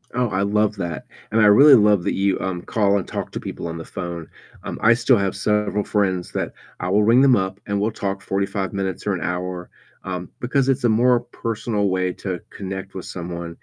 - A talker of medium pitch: No, low, 100 Hz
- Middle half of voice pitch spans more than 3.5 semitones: No, average, 2.8 semitones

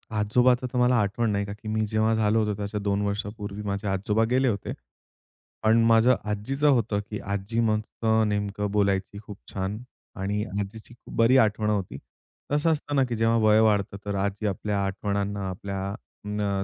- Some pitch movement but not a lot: No, narrow, 1.9 semitones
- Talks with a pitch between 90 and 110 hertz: Yes, low, 105 Hz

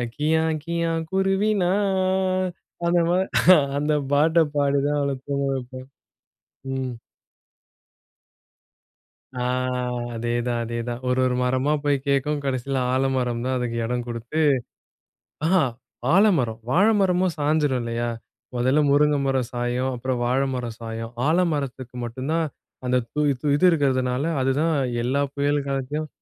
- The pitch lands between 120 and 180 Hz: Yes, medium, 140 Hz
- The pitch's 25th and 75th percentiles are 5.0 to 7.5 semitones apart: No, average, 4.2 semitones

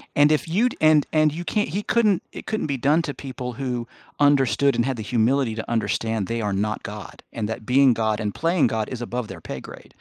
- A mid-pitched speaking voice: No, low, 125 Hz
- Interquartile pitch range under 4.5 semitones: No, average, 5.0 semitones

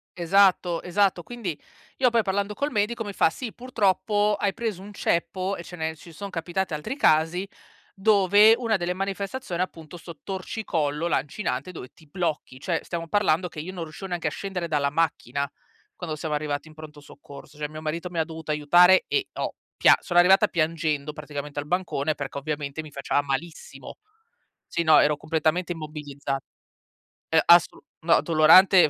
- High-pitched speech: No, medium, 170 Hz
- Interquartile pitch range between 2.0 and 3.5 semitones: No, average, 4.0 semitones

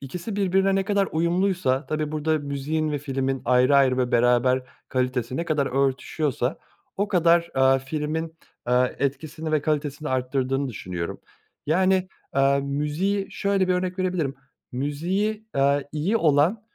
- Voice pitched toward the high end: No, medium, 150 Hz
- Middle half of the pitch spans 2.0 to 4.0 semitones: No, average, 5.0 semitones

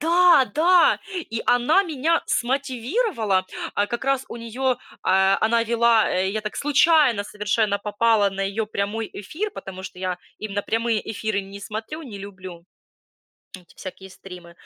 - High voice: Yes, high, 220 Hz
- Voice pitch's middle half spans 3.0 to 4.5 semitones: No, average, 5.2 semitones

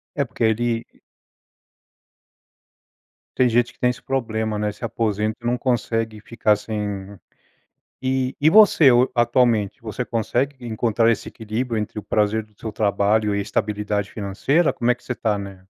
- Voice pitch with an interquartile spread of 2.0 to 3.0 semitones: Yes, narrow, 2.6 semitones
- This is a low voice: Yes, low, 110 Hz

